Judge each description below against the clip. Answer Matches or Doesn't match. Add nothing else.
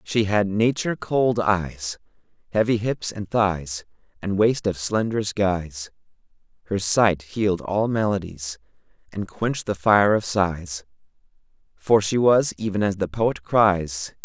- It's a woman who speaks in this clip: Doesn't match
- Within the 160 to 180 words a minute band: Doesn't match